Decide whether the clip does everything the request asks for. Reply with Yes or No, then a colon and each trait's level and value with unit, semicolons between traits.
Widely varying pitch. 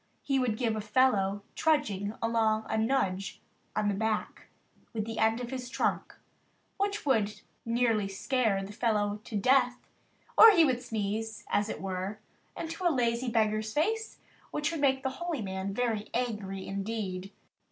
No: average, 4.0 semitones